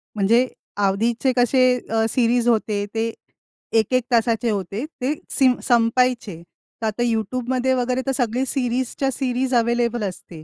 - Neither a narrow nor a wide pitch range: No, narrow, 2.3 semitones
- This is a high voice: Yes, high, 240 Hz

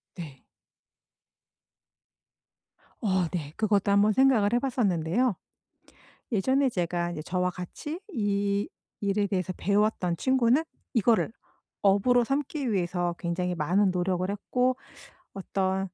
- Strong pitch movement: No, average, 4.6 semitones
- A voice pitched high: Yes, high, 200 Hz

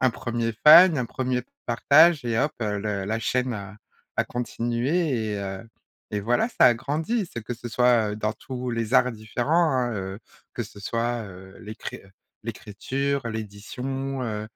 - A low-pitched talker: Yes, low, 120 Hz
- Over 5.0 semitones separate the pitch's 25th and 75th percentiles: No, average, 3.4 semitones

